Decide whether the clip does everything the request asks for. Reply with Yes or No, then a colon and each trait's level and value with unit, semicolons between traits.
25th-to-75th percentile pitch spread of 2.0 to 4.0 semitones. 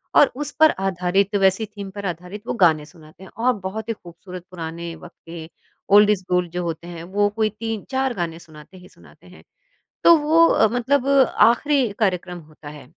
No: average, 4.7 semitones